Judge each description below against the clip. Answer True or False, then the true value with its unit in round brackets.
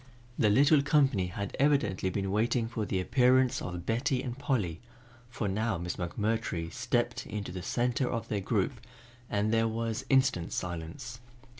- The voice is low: True (115 Hz)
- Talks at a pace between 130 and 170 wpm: True (155 wpm)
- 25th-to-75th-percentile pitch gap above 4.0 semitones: True (4.7 semitones)